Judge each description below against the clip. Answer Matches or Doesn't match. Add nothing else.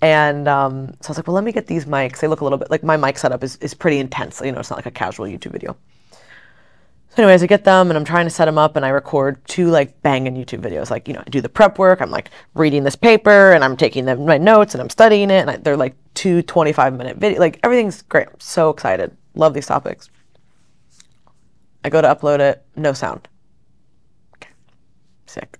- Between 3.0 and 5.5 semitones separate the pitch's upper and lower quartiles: Matches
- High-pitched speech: Doesn't match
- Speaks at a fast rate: Matches